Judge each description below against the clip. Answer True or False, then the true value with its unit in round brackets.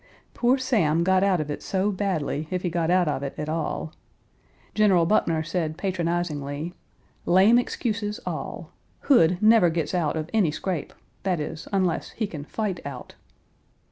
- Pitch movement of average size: True (3.9 semitones)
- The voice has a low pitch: False (175 Hz)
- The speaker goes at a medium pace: True (160 wpm)